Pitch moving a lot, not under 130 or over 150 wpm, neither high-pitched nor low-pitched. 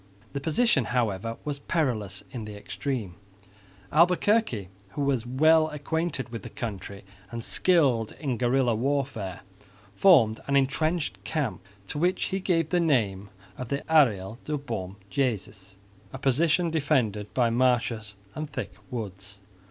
No: wide, 5.9 semitones; slow, 135 wpm; low, 130 Hz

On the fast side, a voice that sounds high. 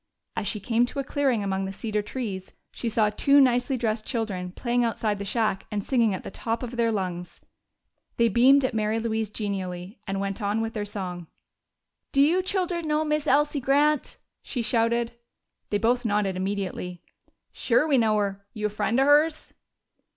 No: average, 185 wpm; high, 225 Hz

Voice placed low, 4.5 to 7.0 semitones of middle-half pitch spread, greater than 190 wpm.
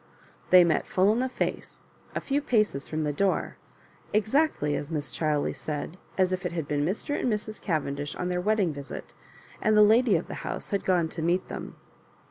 No: medium, 180 Hz; wide, 5.6 semitones; average, 200 wpm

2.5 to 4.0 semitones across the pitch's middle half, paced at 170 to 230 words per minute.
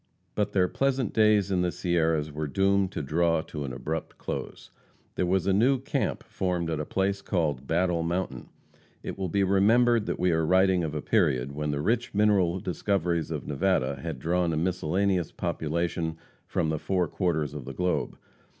Yes: average, 3.6 semitones; average, 185 wpm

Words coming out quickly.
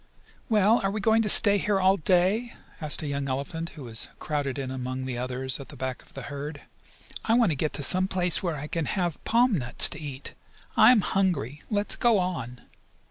Yes: fast, 215 wpm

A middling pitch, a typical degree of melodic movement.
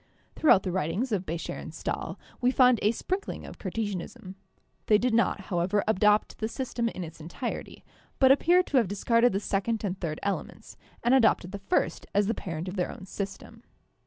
No: high, 210 Hz; average, 4.0 semitones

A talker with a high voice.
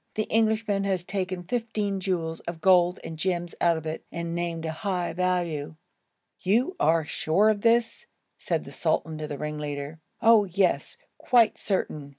No: medium, 180 Hz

